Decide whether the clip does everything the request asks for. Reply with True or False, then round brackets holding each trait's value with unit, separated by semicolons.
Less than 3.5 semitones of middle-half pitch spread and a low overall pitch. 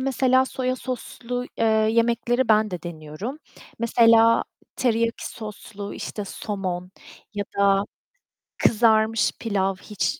False (3.1 semitones; 225 Hz)